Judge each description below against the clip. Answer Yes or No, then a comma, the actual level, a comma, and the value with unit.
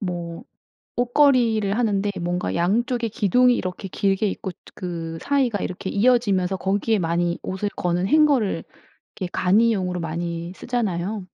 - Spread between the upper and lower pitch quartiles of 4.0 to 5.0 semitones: Yes, average, 4.5 semitones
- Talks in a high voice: Yes, high, 195 Hz